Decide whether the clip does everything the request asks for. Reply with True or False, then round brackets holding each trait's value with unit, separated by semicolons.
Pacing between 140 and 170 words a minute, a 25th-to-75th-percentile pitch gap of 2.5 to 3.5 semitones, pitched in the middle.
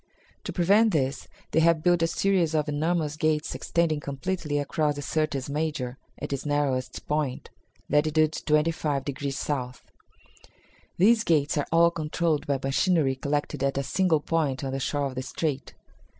True (160 wpm; 2.9 semitones; 150 Hz)